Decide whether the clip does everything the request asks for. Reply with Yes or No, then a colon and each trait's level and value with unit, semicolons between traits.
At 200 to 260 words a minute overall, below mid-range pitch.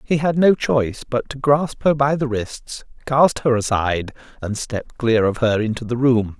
Yes: fast, 205 wpm; low, 125 Hz